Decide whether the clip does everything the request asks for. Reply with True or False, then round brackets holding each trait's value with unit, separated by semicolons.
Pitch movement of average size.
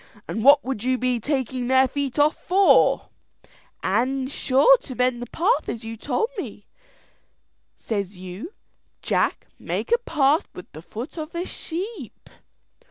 True (4.5 semitones)